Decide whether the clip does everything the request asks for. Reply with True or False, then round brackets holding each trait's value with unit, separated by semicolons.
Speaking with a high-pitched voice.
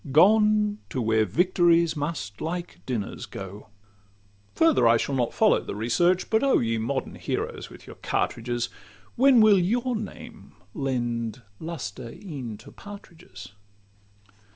False (145 Hz)